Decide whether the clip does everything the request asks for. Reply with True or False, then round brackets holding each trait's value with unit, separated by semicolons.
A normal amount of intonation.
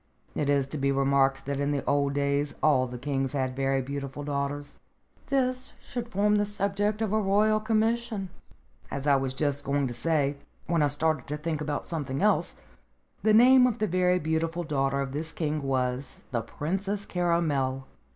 False (6.0 semitones)